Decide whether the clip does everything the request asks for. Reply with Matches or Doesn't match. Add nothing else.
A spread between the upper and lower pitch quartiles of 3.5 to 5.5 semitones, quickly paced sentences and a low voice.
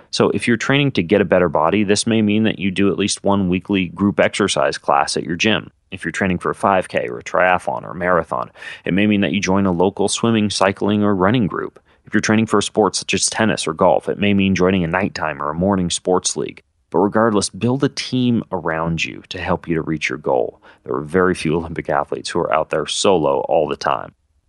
Doesn't match